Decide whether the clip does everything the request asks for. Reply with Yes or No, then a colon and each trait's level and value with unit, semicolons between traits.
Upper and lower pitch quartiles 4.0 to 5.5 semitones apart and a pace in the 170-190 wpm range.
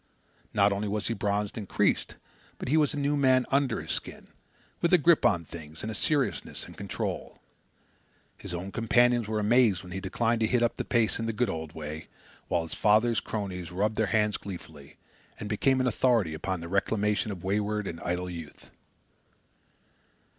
Yes: average, 4.5 semitones; average, 185 wpm